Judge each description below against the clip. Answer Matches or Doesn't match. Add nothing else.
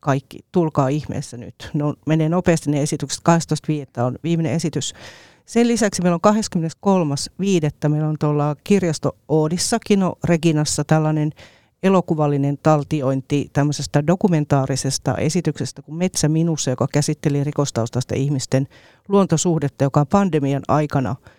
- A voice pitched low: Doesn't match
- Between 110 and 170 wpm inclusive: Matches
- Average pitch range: Matches